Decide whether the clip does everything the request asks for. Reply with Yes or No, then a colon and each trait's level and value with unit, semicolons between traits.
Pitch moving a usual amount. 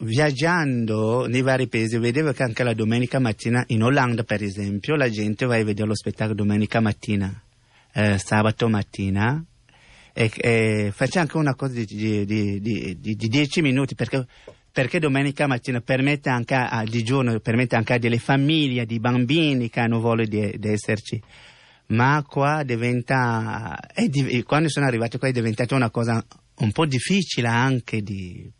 Yes: average, 3.5 semitones